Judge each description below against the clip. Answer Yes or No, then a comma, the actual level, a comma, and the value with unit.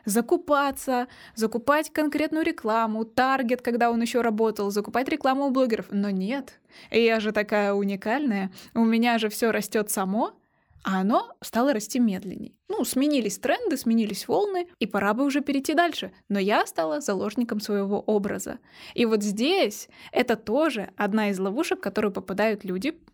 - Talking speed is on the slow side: No, average, 155 wpm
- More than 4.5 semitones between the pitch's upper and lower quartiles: Yes, average, 5.1 semitones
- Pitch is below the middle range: No, high, 230 Hz